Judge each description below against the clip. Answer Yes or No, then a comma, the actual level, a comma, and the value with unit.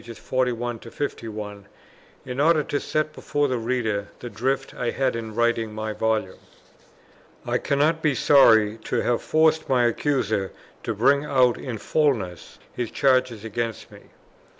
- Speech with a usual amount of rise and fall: Yes, average, 3.9 semitones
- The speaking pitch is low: Yes, low, 120 Hz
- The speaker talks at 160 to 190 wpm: No, average, 145 wpm